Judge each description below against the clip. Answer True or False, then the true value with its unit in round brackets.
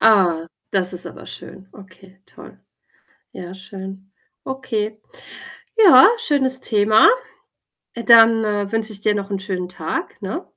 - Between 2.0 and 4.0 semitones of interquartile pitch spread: True (2.9 semitones)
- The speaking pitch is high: True (205 Hz)